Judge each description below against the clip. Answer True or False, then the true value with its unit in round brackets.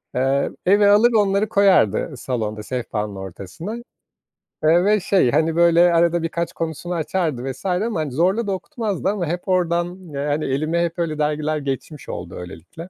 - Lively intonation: False (5.0 semitones)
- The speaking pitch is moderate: True (165 Hz)